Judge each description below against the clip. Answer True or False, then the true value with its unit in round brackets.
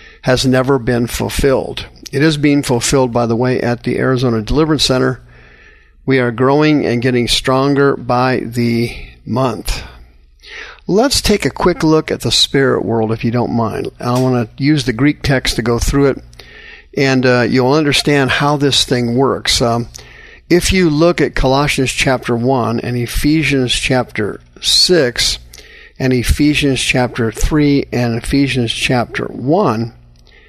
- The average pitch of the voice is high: False (125 Hz)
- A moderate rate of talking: True (150 wpm)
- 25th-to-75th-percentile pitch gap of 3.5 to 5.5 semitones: False (2.9 semitones)